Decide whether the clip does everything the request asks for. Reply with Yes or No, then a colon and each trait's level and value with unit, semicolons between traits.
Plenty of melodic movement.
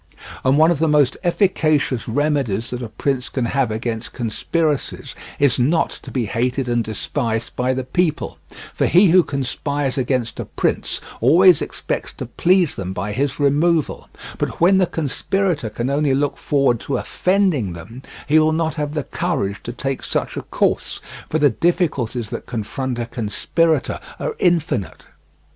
No: average, 4.9 semitones